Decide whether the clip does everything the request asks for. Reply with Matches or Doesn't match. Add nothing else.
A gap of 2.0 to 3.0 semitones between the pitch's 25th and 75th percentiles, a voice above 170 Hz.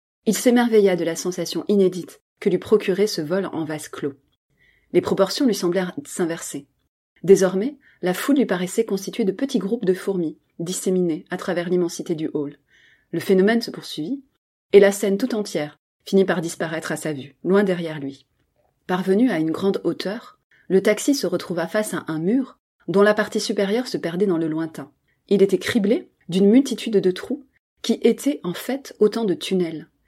Doesn't match